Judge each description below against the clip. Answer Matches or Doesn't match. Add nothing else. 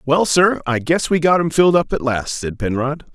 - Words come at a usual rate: Doesn't match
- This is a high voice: Doesn't match